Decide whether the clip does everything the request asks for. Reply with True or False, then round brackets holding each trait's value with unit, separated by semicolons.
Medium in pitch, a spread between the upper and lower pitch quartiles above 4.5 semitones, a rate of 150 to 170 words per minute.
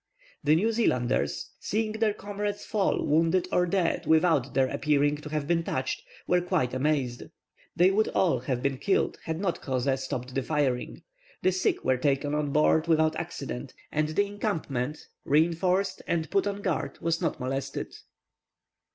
True (155 Hz; 5.2 semitones; 160 wpm)